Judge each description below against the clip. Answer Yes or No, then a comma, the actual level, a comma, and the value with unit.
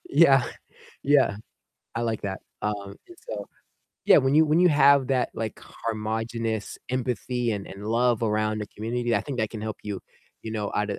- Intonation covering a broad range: No, average, 3.3 semitones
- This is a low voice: Yes, low, 115 Hz